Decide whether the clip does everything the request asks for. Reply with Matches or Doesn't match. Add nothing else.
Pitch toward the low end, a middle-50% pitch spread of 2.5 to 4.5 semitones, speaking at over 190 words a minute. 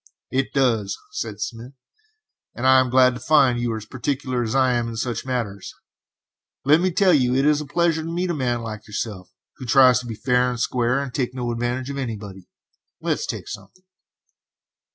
Matches